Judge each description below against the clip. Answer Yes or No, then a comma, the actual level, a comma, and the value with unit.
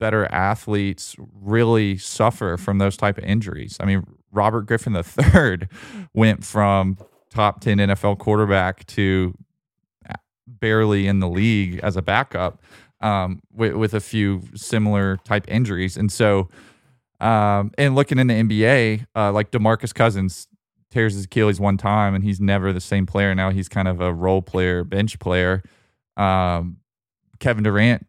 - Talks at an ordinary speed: Yes, average, 150 wpm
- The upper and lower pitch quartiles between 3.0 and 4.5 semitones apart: No, narrow, 2.4 semitones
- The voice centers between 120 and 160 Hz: No, low, 100 Hz